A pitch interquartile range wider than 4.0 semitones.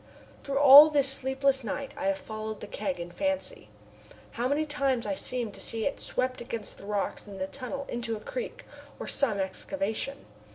Yes: average, 4.7 semitones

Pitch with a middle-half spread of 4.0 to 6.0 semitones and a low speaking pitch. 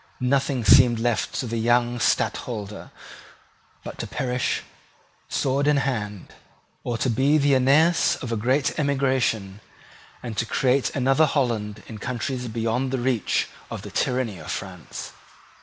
No: average, 3.1 semitones; low, 125 Hz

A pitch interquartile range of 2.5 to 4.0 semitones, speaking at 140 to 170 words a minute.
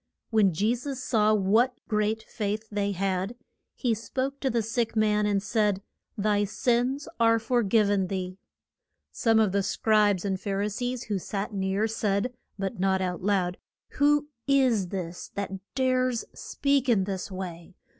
Yes: average, 3.3 semitones; average, 165 wpm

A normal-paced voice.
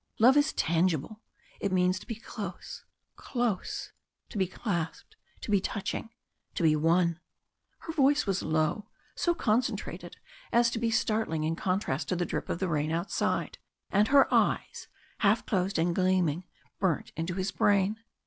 Yes: average, 160 wpm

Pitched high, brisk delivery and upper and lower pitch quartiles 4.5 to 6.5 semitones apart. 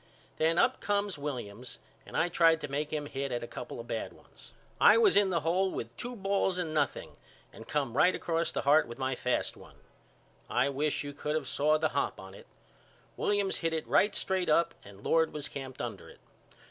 No: medium, 150 Hz; fast, 210 wpm; average, 5.0 semitones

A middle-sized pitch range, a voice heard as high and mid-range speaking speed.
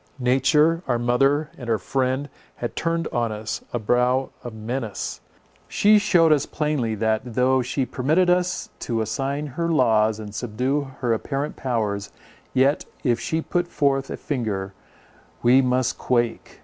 No: average, 3.9 semitones; low, 130 Hz; average, 155 wpm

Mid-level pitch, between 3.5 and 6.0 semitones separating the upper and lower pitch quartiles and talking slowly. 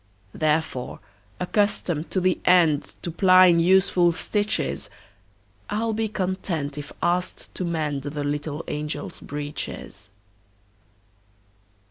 Yes: medium, 165 Hz; average, 4.1 semitones; slow, 90 wpm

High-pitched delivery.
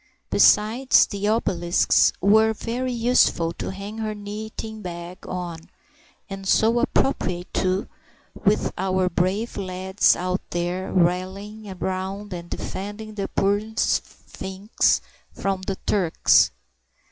Yes: high, 195 Hz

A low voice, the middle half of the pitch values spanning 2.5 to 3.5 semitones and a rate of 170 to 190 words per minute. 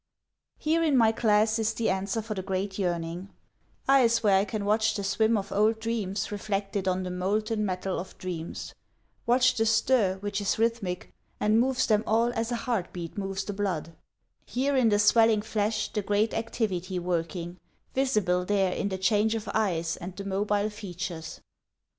No: high, 205 Hz; average, 2.9 semitones; average, 175 wpm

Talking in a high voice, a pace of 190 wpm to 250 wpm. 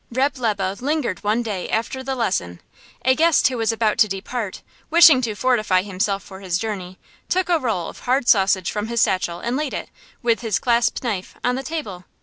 Yes: high, 225 Hz; average, 200 wpm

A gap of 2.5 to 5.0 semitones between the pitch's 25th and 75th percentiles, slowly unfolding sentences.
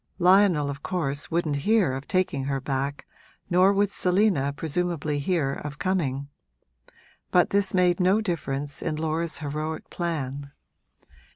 Yes: average, 4.4 semitones; slow, 130 wpm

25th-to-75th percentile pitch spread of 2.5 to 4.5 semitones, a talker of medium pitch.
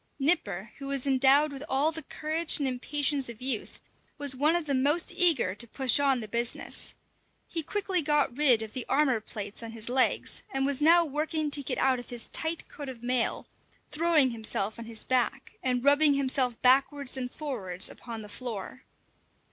No: average, 3.6 semitones; very high, 270 Hz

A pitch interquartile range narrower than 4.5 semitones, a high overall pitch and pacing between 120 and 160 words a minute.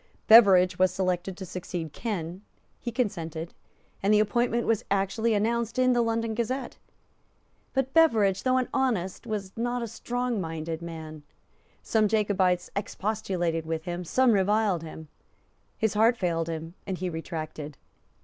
No: average, 4.9 semitones; high, 200 Hz; average, 140 wpm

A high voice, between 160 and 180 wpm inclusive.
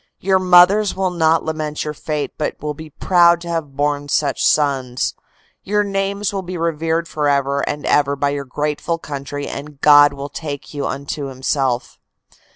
No: medium, 150 Hz; average, 165 wpm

